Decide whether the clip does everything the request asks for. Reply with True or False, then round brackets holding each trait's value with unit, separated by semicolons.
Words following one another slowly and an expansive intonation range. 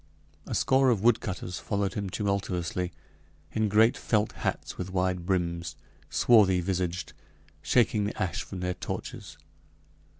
False (130 wpm; 2.8 semitones)